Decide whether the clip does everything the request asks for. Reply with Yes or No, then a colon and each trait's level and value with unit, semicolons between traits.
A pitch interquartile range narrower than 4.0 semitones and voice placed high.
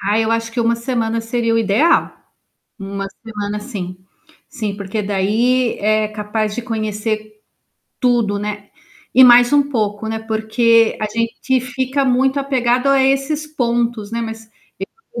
Yes: average, 2.8 semitones; high, 230 Hz